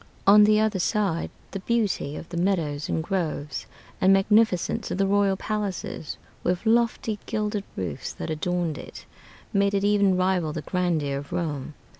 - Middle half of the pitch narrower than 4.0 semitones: No, average, 4.3 semitones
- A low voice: No, high, 190 Hz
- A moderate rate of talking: Yes, average, 160 wpm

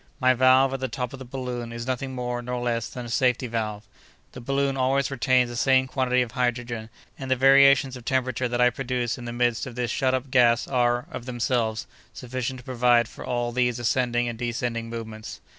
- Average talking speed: No, fast, 210 wpm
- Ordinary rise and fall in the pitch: No, narrow, 1.5 semitones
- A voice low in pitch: Yes, low, 125 Hz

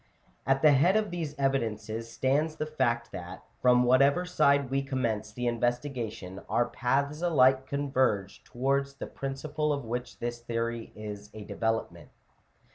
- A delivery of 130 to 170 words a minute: Yes, average, 150 wpm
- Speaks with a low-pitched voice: Yes, low, 130 Hz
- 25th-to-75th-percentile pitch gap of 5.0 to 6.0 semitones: No, average, 3.4 semitones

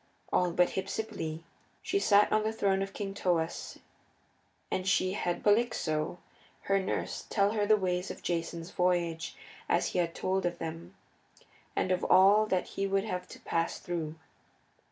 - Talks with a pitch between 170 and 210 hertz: Yes, medium, 185 Hz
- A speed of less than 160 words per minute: No, average, 165 wpm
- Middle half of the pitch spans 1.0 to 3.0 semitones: Yes, narrow, 2.6 semitones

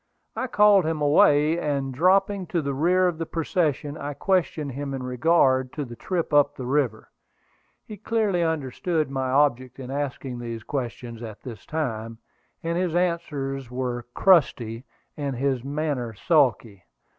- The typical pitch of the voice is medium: Yes, medium, 145 Hz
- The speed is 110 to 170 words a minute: Yes, average, 155 wpm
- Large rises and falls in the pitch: No, average, 4.6 semitones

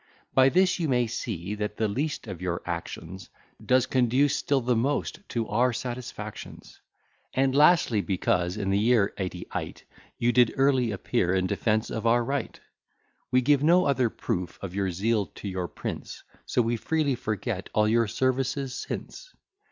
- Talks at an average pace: Yes, average, 165 wpm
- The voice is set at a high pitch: No, low, 115 Hz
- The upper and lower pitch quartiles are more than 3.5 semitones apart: Yes, average, 4.7 semitones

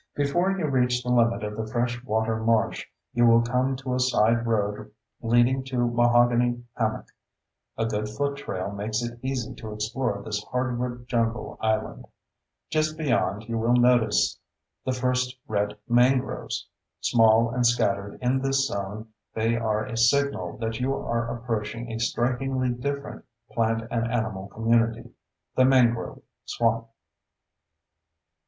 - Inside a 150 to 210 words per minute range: No, average, 140 wpm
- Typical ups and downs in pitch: No, narrow, 2.1 semitones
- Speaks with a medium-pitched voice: No, low, 120 Hz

